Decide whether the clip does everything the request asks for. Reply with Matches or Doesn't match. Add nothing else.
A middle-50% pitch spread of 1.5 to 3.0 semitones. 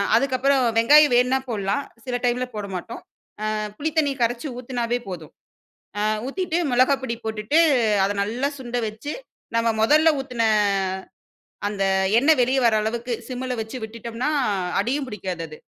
Doesn't match